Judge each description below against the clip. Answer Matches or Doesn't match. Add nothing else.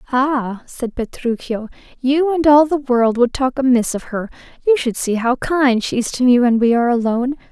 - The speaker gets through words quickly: Matches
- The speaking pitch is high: Matches